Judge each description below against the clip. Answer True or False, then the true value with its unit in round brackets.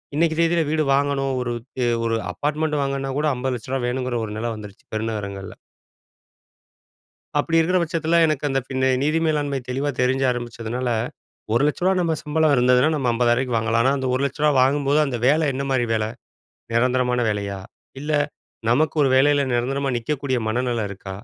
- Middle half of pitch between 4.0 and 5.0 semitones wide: False (3.5 semitones)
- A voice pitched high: False (130 Hz)